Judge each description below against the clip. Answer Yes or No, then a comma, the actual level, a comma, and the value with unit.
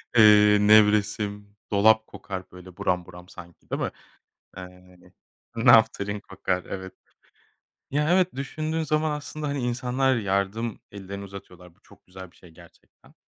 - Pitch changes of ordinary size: Yes, average, 4.7 semitones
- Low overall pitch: Yes, low, 105 Hz